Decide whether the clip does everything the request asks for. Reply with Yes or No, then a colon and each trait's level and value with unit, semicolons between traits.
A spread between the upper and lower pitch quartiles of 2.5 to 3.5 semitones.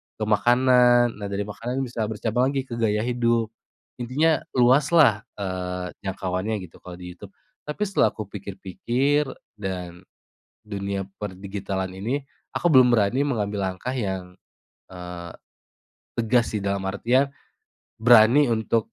No: average, 4.2 semitones